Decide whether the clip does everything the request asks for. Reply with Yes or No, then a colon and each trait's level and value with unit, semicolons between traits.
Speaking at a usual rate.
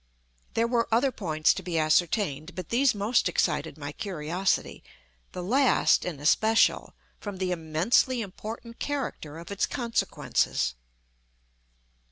No: slow, 120 wpm